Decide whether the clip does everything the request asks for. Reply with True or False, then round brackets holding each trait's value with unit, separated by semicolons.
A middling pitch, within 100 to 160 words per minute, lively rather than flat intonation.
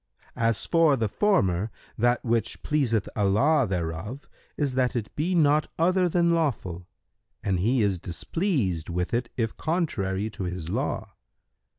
False (115 Hz; 145 wpm; 8.1 semitones)